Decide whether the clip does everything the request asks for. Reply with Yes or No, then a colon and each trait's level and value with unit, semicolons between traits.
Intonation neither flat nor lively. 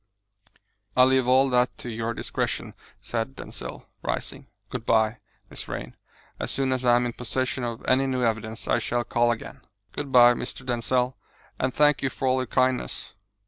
No: narrow, 1.6 semitones